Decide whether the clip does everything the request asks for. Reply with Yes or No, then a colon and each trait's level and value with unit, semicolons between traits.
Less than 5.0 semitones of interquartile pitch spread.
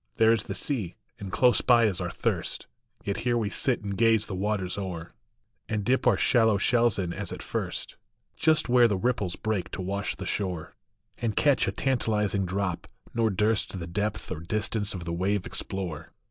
Yes: average, 3.5 semitones